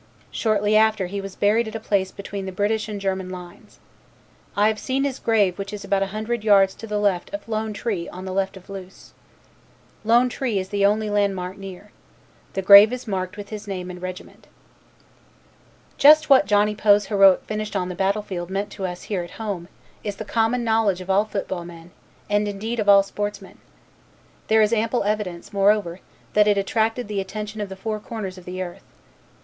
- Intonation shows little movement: Yes, narrow, 2.1 semitones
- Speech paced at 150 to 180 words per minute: No, average, 200 wpm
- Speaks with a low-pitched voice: No, high, 205 Hz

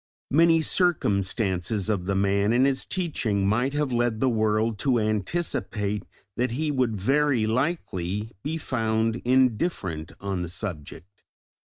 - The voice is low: Yes, low, 110 Hz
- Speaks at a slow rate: Yes, slow, 130 wpm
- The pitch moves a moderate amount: Yes, average, 4.9 semitones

